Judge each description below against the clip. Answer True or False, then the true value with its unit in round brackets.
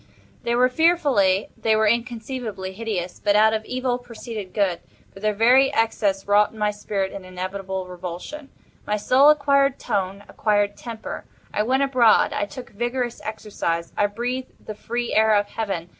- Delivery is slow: False (160 wpm)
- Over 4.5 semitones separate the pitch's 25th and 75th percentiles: False (3.5 semitones)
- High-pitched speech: True (215 Hz)